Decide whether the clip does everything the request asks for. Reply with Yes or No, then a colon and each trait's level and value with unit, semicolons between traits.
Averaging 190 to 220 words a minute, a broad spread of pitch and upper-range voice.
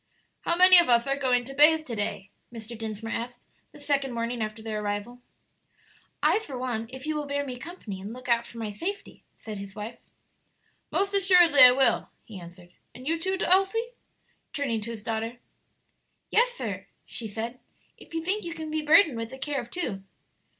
Yes: average, 195 wpm; wide, 6.0 semitones; very high, 250 Hz